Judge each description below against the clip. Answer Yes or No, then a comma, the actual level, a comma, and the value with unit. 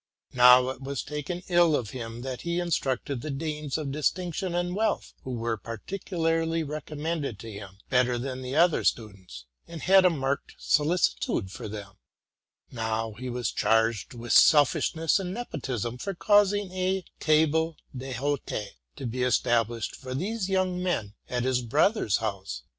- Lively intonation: Yes, wide, 6.4 semitones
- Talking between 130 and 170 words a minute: Yes, average, 155 wpm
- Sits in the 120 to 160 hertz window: Yes, low, 135 Hz